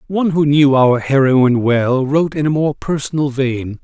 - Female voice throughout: No, male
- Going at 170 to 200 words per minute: Yes, average, 190 wpm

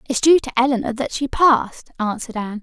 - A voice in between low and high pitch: No, very high, 250 Hz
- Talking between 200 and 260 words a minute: Yes, fast, 205 wpm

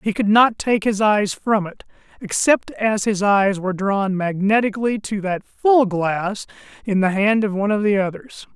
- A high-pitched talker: Yes, high, 205 Hz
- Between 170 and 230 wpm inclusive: Yes, average, 180 wpm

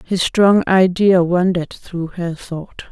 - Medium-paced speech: Yes, average, 145 wpm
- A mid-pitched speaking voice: Yes, medium, 180 Hz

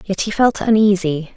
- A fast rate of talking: No, average, 175 wpm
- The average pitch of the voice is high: Yes, high, 200 Hz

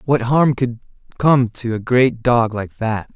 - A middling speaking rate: Yes, average, 190 wpm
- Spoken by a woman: No, male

